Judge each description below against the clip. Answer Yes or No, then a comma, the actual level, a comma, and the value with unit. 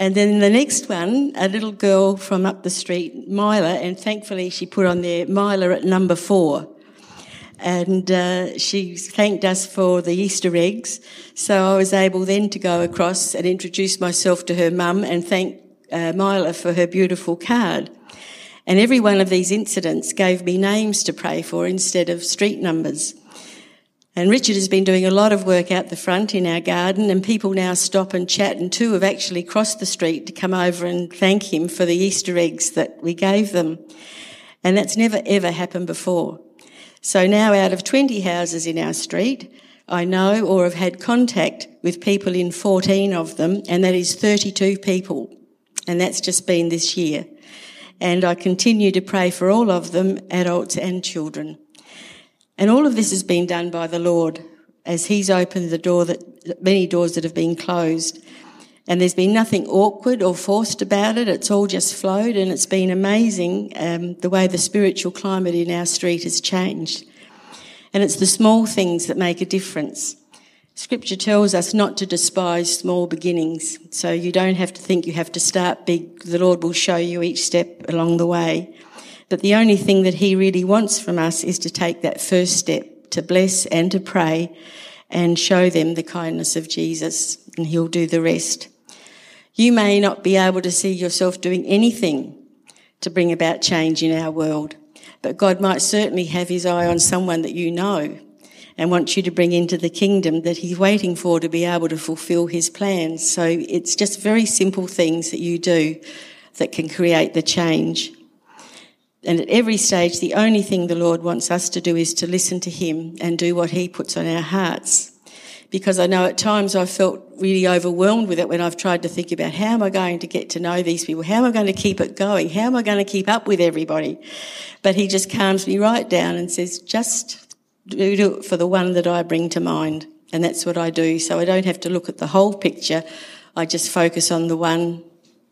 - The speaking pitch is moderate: Yes, medium, 180 Hz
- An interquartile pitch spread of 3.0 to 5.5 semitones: No, narrow, 2.4 semitones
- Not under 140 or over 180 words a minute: No, average, 200 wpm